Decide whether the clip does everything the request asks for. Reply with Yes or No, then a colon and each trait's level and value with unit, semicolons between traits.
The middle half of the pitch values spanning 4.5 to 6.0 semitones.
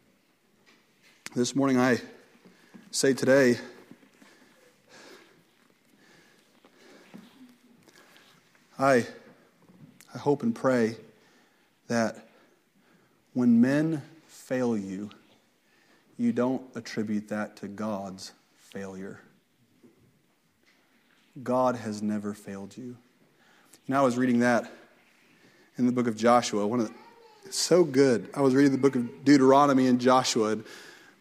No: average, 3.9 semitones